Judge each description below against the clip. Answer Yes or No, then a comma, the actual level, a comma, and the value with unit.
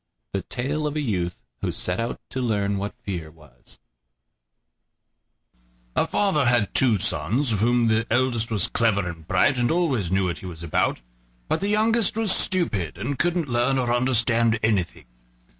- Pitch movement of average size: No, wide, 5.8 semitones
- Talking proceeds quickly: No, average, 170 wpm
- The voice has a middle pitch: No, low, 115 Hz